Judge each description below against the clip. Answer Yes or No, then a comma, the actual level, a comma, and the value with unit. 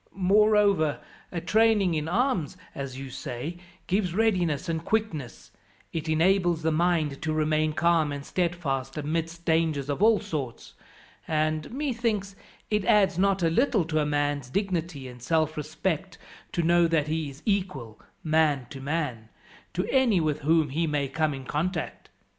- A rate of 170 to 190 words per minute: No, average, 155 wpm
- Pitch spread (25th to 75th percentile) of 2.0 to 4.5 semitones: Yes, average, 4.1 semitones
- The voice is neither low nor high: Yes, medium, 160 Hz